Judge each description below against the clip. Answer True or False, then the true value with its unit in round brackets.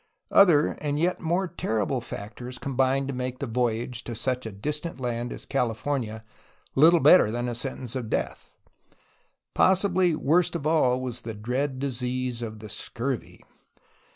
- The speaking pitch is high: False (130 Hz)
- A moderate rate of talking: True (155 wpm)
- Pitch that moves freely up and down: False (3.7 semitones)